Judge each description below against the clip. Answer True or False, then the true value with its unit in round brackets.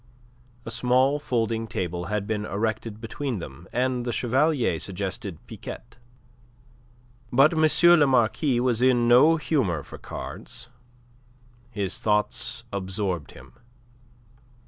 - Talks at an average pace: False (115 wpm)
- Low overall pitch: True (115 Hz)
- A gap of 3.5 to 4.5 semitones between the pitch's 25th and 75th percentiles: True (4.2 semitones)